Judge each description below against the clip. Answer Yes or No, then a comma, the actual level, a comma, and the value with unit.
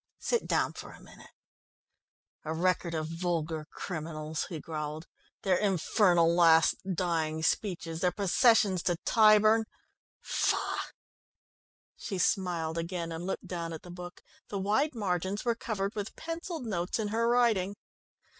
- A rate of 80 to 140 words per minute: Yes, slow, 135 wpm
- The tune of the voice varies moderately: Yes, average, 4.0 semitones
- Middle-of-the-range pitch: Yes, medium, 180 Hz